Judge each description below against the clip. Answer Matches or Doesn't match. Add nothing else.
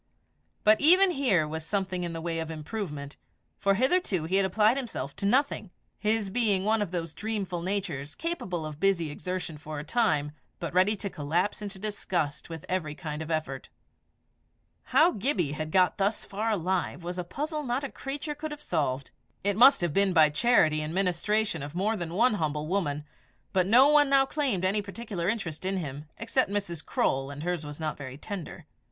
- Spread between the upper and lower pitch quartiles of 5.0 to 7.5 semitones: Matches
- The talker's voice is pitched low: Doesn't match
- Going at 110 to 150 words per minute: Doesn't match